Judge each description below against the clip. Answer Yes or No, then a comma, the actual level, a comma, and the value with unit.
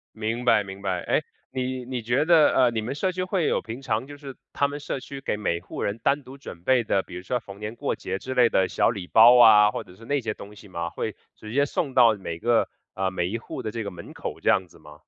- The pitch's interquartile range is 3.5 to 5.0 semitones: Yes, average, 4.7 semitones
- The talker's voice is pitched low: Yes, low, 115 Hz